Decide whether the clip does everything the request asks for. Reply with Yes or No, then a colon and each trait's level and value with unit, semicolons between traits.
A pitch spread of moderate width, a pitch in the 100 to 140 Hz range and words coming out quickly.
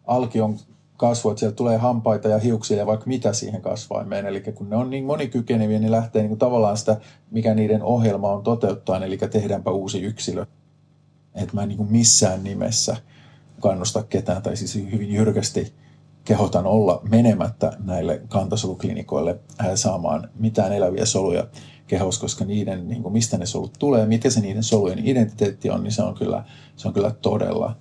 No: narrow, 2.2 semitones; low, 110 Hz; fast, 175 wpm